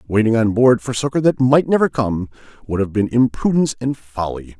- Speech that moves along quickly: No, average, 195 wpm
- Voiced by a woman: No, male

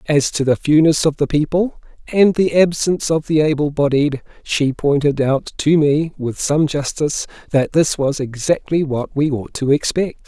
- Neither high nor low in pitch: Yes, medium, 150 Hz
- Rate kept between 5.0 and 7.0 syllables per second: No, 4.6 syllables/s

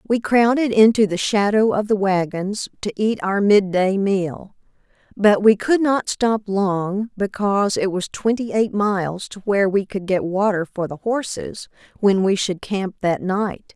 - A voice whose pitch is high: Yes, high, 200 Hz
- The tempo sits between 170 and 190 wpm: Yes, average, 175 wpm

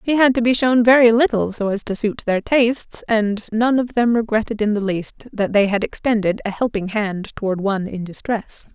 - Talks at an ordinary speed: No, fast, 220 wpm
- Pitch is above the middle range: Yes, high, 220 Hz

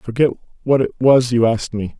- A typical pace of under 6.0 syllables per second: No, 6.7 syllables/s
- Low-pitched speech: Yes, low, 120 Hz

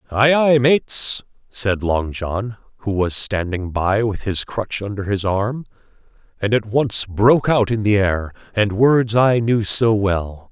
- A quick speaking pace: No, average, 170 wpm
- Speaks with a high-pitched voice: No, low, 105 Hz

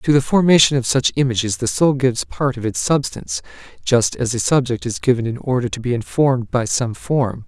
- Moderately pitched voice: No, low, 125 Hz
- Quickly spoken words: Yes, fast, 215 wpm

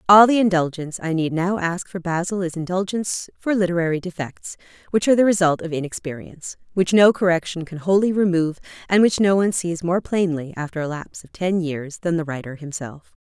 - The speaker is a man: No, female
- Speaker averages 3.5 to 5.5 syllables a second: No, 5.9 syllables/s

